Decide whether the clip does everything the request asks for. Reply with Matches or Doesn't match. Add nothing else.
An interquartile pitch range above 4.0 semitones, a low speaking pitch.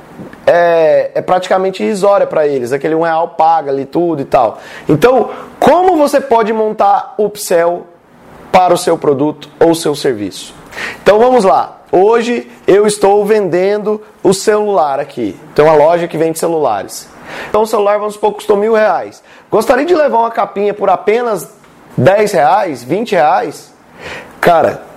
Doesn't match